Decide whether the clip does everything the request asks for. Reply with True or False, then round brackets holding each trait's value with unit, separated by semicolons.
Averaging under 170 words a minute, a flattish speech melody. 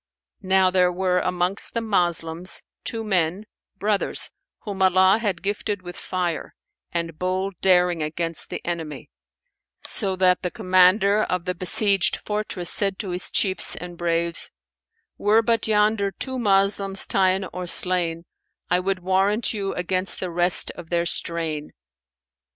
True (140 wpm; 2.2 semitones)